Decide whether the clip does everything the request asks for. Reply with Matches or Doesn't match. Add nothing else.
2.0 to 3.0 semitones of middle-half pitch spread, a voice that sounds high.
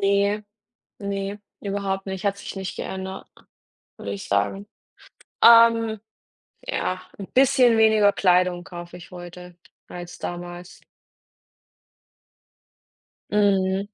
Matches